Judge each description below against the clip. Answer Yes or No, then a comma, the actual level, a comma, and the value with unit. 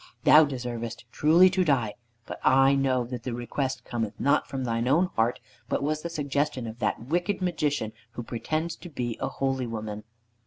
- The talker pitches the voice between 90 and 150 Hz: Yes, low, 135 Hz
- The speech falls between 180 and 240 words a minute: Yes, average, 185 wpm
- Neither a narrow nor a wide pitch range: Yes, average, 4.4 semitones